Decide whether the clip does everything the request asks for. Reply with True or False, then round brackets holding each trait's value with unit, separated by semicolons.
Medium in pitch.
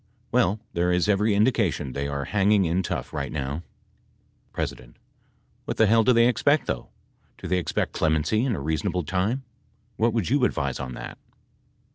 False (95 Hz)